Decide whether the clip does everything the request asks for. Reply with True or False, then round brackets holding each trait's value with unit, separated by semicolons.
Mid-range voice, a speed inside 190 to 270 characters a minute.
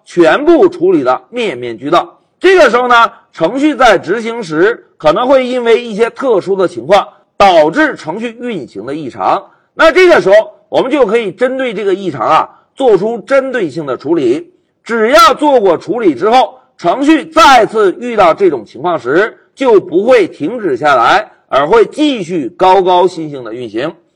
False (300 Hz; 255 characters per minute)